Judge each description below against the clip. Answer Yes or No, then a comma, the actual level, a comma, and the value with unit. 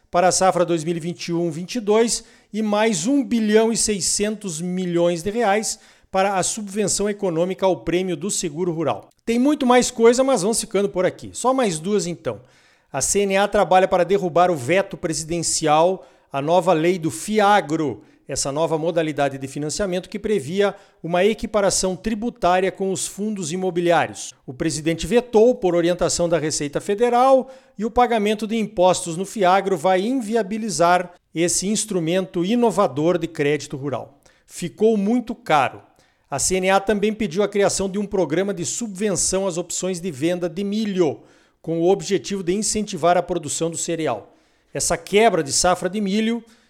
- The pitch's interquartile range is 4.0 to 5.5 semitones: No, average, 3.6 semitones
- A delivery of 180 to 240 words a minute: No, average, 155 wpm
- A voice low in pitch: No, medium, 185 Hz